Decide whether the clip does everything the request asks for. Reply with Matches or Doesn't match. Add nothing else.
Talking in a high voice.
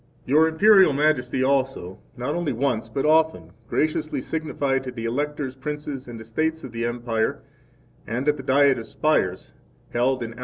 Doesn't match